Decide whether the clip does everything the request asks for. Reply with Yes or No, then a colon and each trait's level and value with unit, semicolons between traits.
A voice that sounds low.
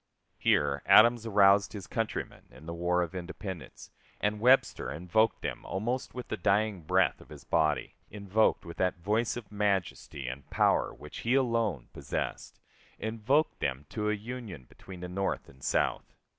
Yes: low, 100 Hz